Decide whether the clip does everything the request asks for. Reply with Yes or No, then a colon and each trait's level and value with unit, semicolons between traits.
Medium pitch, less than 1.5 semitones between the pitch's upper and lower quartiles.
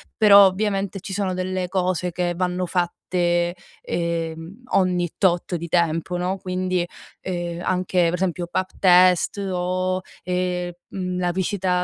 Yes: medium, 180 Hz; narrow, 1.1 semitones